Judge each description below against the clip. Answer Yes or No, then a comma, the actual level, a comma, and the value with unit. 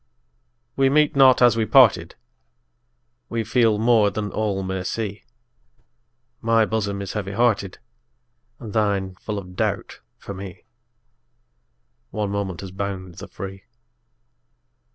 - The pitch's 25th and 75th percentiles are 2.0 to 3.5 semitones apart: Yes, average, 2.7 semitones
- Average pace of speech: No, slow, 125 wpm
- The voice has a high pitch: No, low, 105 Hz